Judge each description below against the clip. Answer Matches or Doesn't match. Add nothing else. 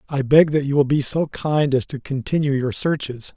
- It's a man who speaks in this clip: Matches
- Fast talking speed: Matches